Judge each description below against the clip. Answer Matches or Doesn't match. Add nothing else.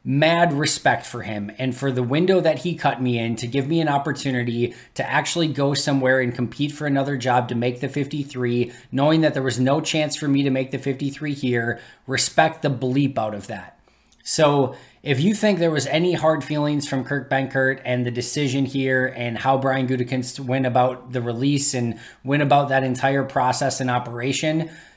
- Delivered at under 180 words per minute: Doesn't match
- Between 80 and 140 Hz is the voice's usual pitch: Matches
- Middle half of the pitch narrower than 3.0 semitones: Matches